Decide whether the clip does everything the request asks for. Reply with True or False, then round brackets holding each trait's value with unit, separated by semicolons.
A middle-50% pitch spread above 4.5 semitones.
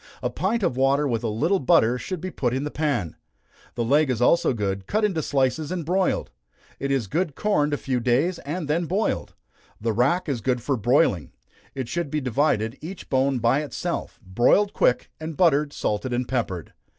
True (5.0 semitones)